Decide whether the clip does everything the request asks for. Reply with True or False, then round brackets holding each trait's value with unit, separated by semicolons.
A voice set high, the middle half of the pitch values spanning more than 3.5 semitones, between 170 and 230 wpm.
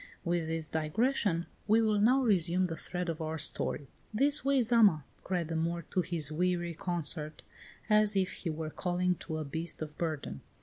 False (175 Hz; 4.2 semitones; 180 wpm)